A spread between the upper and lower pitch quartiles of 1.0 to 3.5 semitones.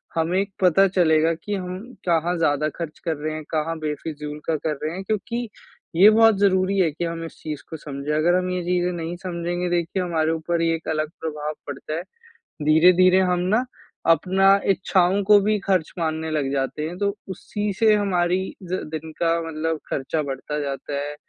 Yes: average, 3.1 semitones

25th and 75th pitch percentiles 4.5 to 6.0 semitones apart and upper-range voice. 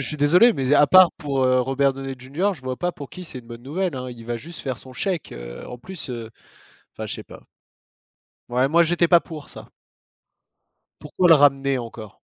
No: average, 4.9 semitones; low, 135 Hz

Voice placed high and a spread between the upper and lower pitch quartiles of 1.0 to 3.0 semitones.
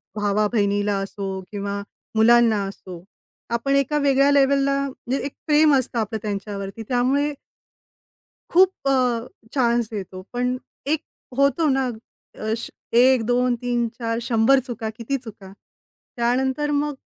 No: high, 240 Hz; average, 4.0 semitones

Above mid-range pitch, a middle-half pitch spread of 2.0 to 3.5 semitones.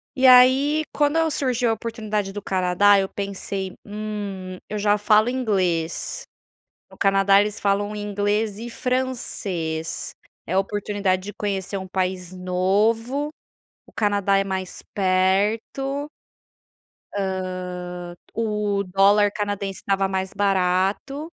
Yes: high, 205 Hz; narrow, 2.6 semitones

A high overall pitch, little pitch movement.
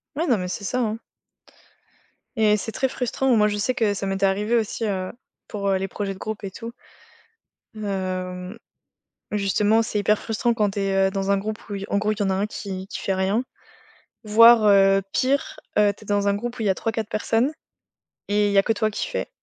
Yes: high, 205 Hz; narrow, 2.3 semitones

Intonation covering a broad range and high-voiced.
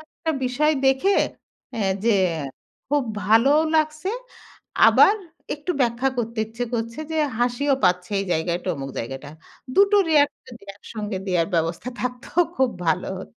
Yes: wide, 7.2 semitones; high, 240 Hz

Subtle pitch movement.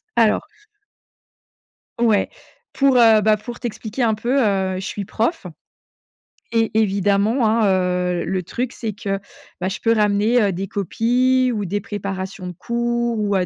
No: average, 3.3 semitones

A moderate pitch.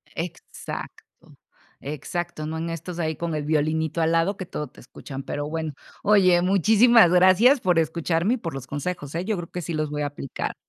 Yes: medium, 165 Hz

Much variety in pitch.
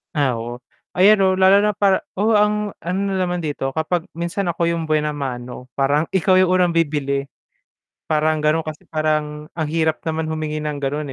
No: average, 3.6 semitones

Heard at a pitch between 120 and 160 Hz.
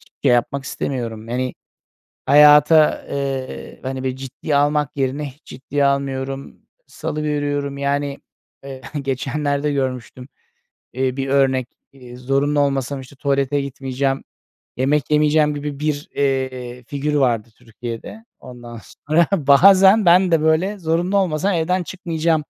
Yes: medium, 140 Hz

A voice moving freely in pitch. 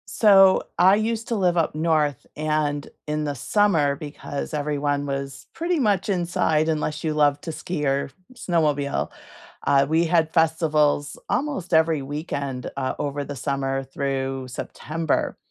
No: average, 3.1 semitones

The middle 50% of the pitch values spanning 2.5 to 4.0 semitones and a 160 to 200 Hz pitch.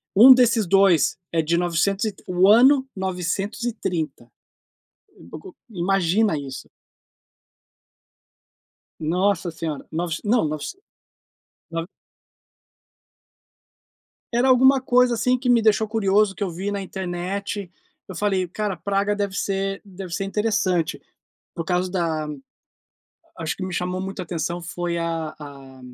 Yes: average, 3.6 semitones; high, 190 Hz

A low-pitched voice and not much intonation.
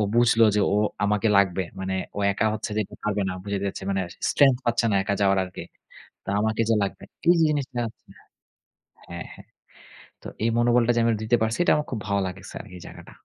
No: low, 110 Hz; average, 3.2 semitones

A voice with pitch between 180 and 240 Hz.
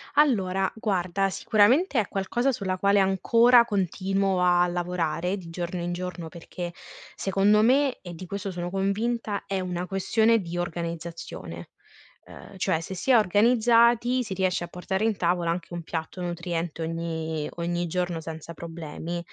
Yes: medium, 185 Hz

